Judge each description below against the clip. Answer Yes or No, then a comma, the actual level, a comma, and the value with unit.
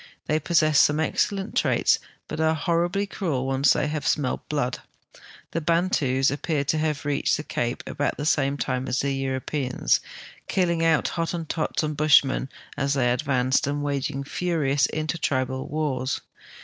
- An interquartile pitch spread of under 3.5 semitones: Yes, average, 2.8 semitones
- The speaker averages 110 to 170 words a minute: Yes, average, 160 wpm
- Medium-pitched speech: Yes, medium, 145 Hz